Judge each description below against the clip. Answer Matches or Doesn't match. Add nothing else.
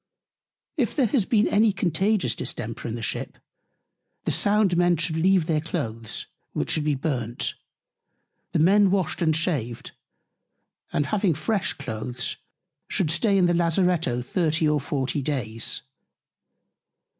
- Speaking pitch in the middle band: Matches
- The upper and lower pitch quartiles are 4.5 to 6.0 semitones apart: Matches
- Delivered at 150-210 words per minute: Doesn't match